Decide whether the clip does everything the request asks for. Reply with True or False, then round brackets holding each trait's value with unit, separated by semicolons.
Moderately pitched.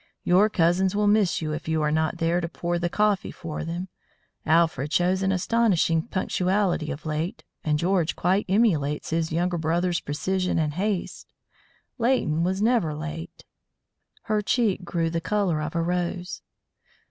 True (175 Hz)